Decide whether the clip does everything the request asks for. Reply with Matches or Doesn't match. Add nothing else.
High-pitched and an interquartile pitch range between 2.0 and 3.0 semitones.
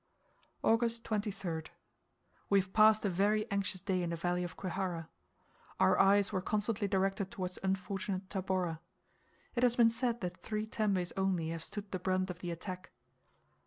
Matches